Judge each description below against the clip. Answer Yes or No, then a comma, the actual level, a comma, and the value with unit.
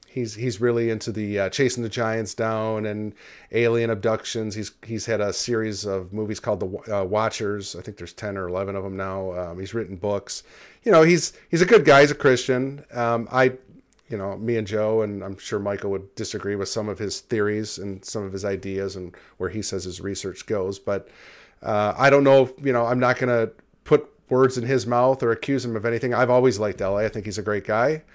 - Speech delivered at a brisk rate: Yes, fast, 230 wpm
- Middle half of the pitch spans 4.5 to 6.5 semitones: No, average, 3.5 semitones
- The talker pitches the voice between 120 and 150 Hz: No, low, 110 Hz